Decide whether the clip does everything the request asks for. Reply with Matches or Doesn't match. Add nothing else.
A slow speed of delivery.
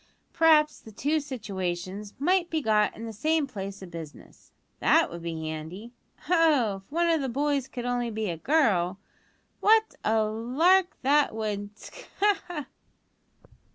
Doesn't match